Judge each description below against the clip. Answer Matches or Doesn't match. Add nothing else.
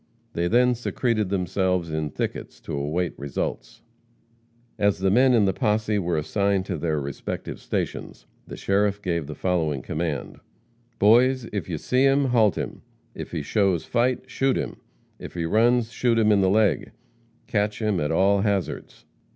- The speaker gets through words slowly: Doesn't match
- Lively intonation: Doesn't match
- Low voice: Matches